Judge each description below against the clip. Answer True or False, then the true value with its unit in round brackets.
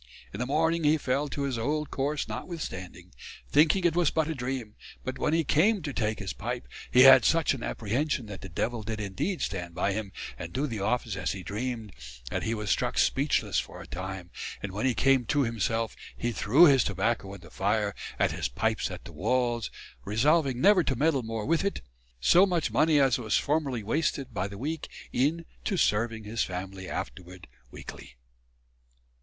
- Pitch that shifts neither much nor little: False (6.3 semitones)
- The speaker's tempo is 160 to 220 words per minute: True (195 wpm)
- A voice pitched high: False (120 Hz)